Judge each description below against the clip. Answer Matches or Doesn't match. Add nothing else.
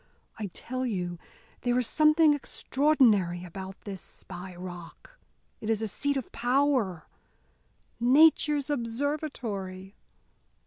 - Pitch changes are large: Matches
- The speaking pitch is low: Doesn't match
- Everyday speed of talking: Doesn't match